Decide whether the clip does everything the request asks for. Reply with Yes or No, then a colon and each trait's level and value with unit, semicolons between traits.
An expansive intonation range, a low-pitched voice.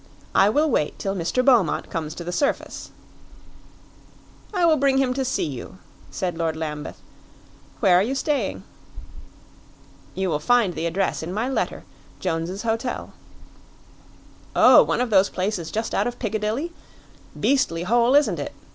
No: wide, 7.0 semitones; high, 210 Hz